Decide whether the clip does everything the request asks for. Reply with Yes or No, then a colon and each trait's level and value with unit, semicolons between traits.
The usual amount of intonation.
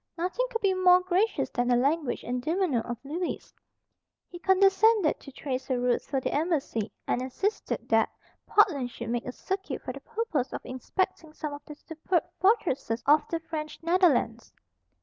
No: wide, 6.4 semitones